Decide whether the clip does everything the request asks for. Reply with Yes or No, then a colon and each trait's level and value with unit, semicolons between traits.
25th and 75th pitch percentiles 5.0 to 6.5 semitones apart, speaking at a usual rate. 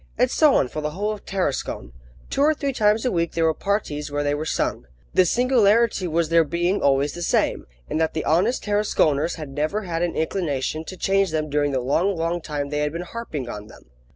No: wide, 5.4 semitones; fast, 225 wpm